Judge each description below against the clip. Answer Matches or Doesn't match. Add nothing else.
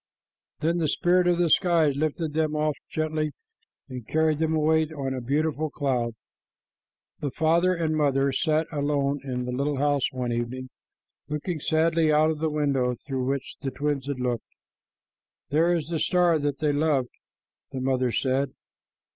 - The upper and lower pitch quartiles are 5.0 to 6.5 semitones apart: Doesn't match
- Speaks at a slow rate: Doesn't match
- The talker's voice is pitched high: Doesn't match